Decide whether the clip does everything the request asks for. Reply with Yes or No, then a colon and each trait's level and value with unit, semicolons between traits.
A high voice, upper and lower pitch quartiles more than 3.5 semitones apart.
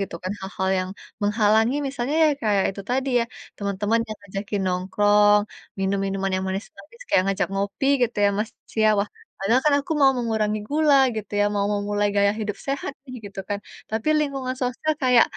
Yes: high, 210 Hz; average, 3.9 semitones